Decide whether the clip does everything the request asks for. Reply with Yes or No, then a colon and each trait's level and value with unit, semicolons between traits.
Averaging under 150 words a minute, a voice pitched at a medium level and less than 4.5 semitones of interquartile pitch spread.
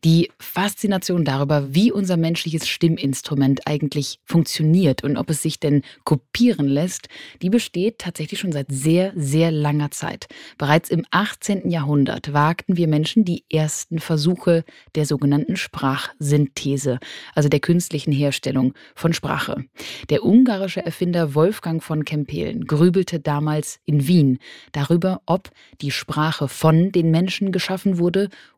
Yes: average, 130 wpm; medium, 160 Hz; average, 3.3 semitones